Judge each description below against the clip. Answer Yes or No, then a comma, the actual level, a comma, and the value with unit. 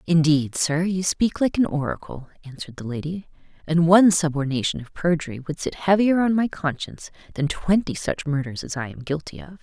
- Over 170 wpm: Yes, average, 185 wpm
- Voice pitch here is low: No, medium, 160 Hz